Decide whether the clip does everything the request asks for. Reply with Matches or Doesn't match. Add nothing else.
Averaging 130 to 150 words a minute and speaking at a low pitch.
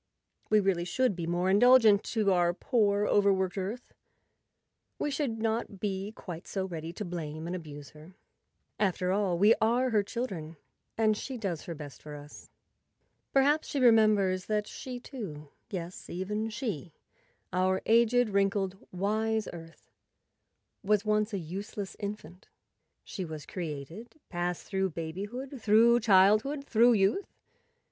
Doesn't match